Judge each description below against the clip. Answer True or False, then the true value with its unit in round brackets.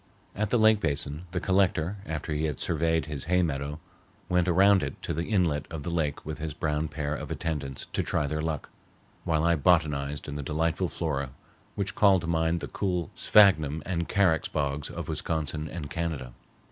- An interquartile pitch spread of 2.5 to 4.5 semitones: True (3.1 semitones)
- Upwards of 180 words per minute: True (190 wpm)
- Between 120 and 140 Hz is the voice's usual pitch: False (80 Hz)